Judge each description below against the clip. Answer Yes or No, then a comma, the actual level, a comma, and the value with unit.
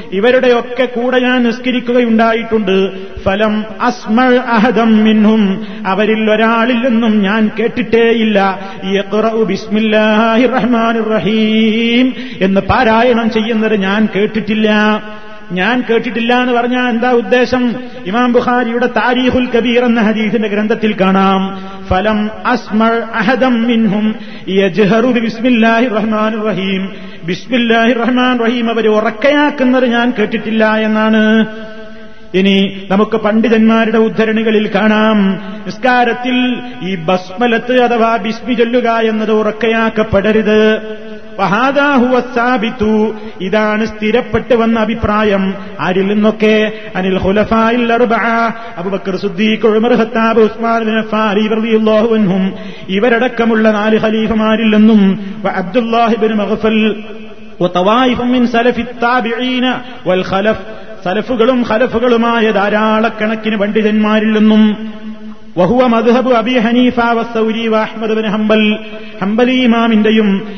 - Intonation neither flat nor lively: No, narrow, 1.6 semitones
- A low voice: No, high, 220 Hz